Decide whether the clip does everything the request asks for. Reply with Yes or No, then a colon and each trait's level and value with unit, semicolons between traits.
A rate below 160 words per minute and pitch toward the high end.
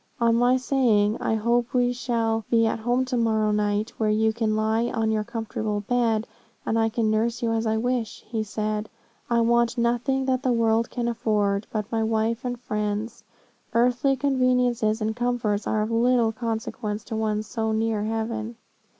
No: average, 180 wpm; high, 225 Hz